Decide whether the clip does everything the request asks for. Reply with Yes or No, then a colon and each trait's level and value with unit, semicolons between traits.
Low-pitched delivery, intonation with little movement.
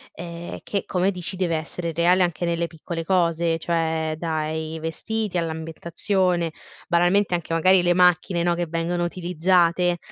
No: medium, 170 Hz; narrow, 1.5 semitones